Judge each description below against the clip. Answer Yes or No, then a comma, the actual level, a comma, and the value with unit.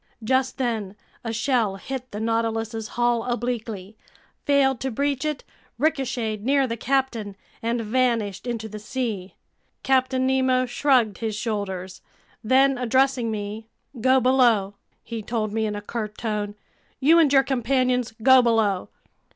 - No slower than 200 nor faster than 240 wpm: No, average, 140 wpm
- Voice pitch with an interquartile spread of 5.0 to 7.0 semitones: No, average, 3.3 semitones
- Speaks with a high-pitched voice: Yes, high, 235 Hz